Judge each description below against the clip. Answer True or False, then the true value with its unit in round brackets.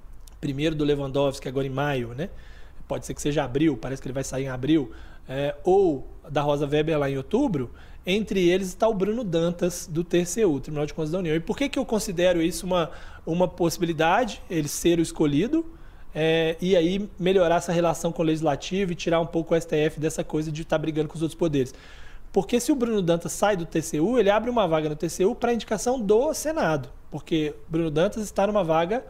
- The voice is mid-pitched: True (165 Hz)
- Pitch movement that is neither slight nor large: True (4.0 semitones)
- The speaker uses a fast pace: True (210 wpm)